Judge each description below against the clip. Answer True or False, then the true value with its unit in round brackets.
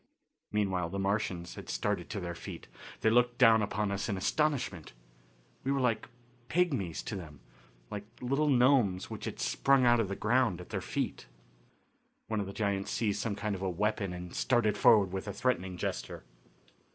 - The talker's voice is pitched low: True (105 Hz)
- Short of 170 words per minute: False (180 wpm)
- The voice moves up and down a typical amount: True (4.4 semitones)